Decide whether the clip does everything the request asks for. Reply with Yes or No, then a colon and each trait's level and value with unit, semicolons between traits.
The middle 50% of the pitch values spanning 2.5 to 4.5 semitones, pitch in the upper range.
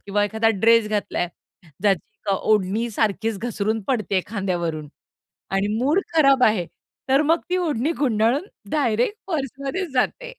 No: average, 5.2 semitones; high, 225 Hz